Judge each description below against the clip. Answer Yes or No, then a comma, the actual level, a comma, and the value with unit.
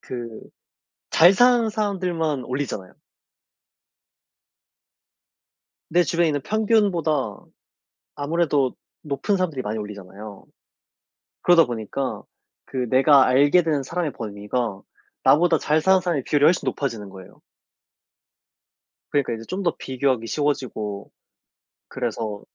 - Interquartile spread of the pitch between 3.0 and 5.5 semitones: No, wide, 6.7 semitones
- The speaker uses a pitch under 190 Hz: Yes, medium, 140 Hz